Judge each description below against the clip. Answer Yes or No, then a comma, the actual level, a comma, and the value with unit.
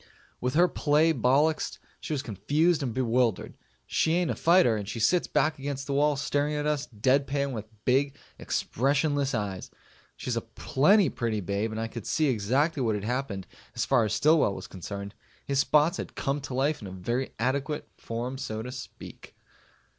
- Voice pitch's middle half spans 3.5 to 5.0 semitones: Yes, average, 4.6 semitones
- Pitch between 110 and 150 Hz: Yes, low, 135 Hz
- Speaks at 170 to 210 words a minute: Yes, average, 185 wpm